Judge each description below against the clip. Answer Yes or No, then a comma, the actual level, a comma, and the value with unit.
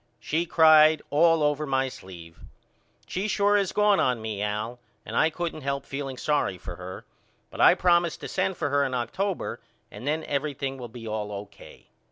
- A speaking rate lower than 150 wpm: No, average, 185 wpm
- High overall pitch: No, medium, 140 Hz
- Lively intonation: Yes, wide, 6.1 semitones